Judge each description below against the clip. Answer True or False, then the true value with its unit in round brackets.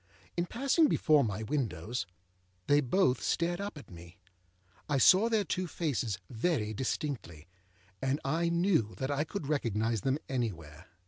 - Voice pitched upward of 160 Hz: False (135 Hz)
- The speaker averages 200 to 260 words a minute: False (145 wpm)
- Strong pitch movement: True (7.6 semitones)